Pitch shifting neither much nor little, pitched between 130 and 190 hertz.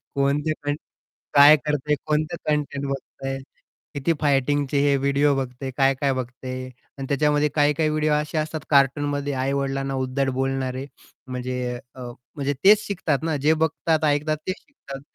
No: narrow, 1.9 semitones; medium, 140 Hz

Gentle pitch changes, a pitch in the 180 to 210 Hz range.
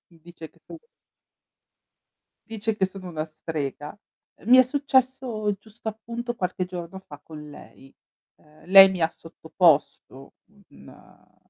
No: wide, 5.7 semitones; medium, 185 Hz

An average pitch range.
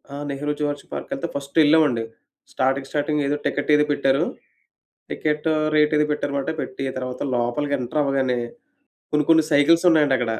No: narrow, 1.9 semitones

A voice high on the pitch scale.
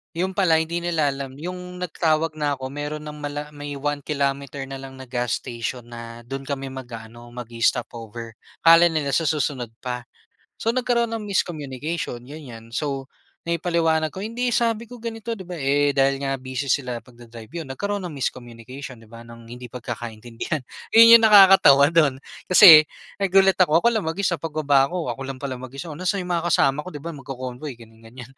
No: medium, 145 Hz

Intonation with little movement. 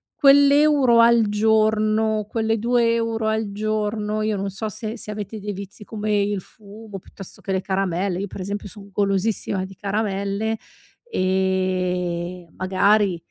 Yes: narrow, 2.3 semitones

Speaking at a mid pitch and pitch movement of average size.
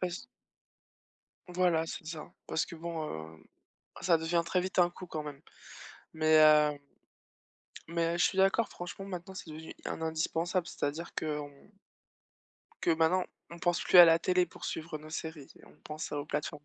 No: medium, 165 Hz; narrow, 2.3 semitones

